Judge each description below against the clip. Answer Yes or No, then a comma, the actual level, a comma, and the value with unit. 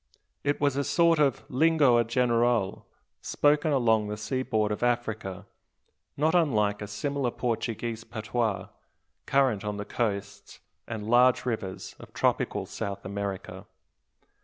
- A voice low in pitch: Yes, low, 115 Hz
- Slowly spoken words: Yes, slow, 125 wpm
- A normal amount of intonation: Yes, average, 4.2 semitones